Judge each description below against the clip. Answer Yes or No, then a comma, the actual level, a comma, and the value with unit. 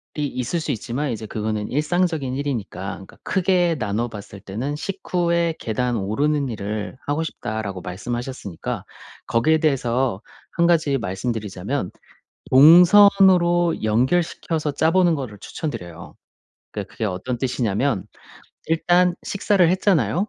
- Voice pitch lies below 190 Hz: Yes, low, 135 Hz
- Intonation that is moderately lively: No, wide, 7.6 semitones